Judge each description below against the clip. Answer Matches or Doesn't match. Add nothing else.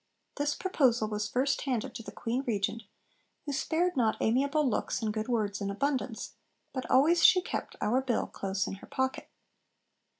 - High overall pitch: Matches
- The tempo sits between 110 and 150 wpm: Doesn't match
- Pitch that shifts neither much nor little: Matches